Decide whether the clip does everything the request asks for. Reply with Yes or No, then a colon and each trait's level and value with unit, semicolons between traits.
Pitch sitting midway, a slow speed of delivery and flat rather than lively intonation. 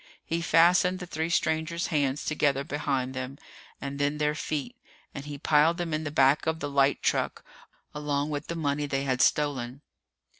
No: medium, 150 Hz; average, 180 wpm; narrow, 2.3 semitones